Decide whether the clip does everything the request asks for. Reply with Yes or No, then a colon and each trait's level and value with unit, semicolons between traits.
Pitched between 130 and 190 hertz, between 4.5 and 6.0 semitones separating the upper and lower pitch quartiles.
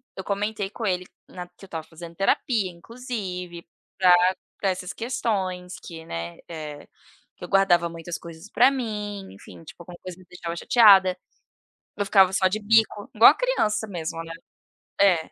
No: medium, 185 Hz; average, 3.4 semitones